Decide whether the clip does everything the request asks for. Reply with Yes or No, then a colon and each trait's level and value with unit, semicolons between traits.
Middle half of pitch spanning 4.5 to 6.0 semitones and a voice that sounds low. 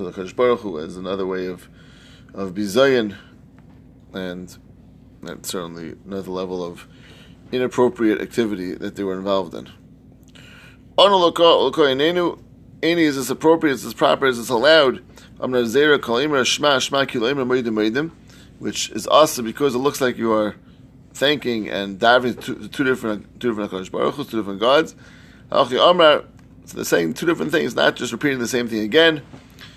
Yes: average, 5.2 semitones; low, 115 Hz